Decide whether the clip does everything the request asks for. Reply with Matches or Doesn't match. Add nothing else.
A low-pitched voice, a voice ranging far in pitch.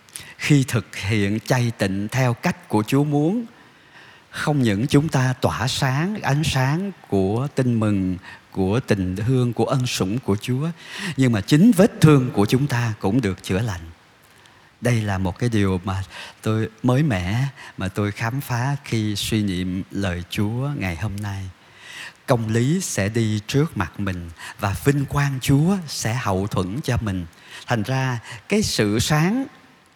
Matches